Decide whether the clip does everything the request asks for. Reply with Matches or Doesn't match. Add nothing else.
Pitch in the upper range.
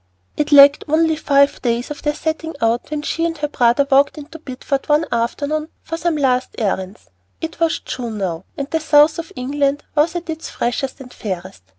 Matches